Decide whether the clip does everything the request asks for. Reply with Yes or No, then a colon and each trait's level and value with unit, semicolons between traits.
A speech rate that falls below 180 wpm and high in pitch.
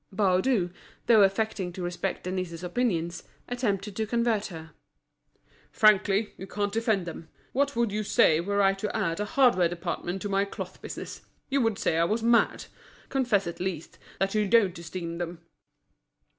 Yes: average, 165 wpm; high, 195 Hz